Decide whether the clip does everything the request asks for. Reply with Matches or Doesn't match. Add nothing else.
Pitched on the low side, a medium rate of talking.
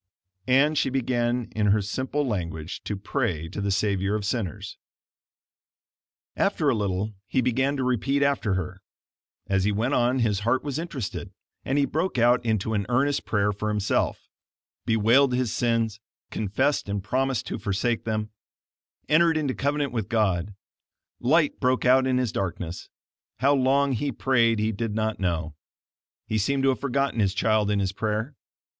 Matches